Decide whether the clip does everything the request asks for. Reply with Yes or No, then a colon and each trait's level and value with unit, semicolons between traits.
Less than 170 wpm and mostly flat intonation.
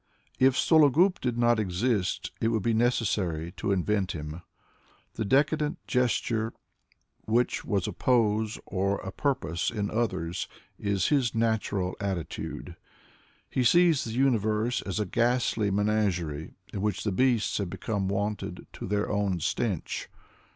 No: slow, 135 wpm; average, 3.8 semitones